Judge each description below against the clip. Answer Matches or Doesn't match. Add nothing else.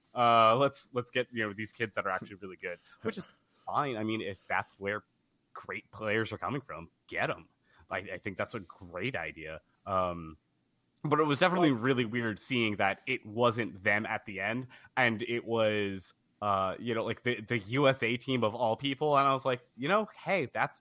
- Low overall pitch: Matches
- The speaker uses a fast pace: Matches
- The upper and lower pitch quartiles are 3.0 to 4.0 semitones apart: Matches